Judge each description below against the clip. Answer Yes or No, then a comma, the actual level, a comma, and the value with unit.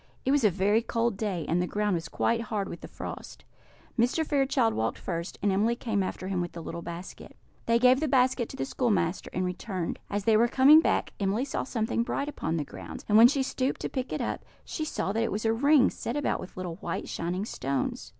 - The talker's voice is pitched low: No, high, 215 Hz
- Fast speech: Yes, fast, 235 wpm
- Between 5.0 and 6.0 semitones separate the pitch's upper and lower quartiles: Yes, wide, 5.6 semitones